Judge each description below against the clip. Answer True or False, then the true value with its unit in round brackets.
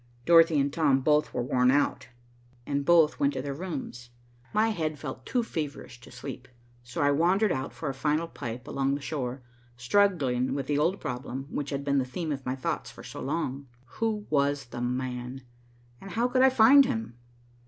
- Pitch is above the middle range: False (140 Hz)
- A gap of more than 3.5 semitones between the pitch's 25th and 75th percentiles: True (4.5 semitones)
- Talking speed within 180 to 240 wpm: True (195 wpm)